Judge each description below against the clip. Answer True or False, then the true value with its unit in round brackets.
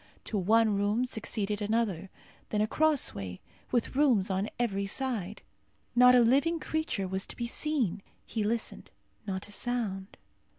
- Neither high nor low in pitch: False (215 Hz)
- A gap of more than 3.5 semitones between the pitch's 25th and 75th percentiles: True (4.0 semitones)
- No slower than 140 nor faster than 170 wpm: True (145 wpm)